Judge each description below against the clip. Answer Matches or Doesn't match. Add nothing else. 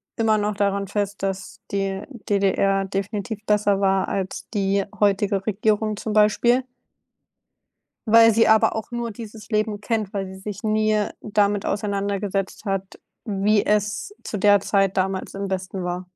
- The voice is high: Matches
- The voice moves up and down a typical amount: Doesn't match